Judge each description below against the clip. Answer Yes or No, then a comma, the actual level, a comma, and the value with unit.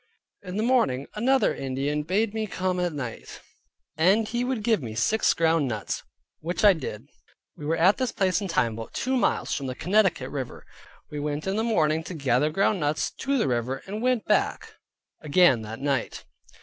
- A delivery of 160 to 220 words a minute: Yes, average, 190 wpm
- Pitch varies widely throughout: Yes, wide, 7.5 semitones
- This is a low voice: No, medium, 165 Hz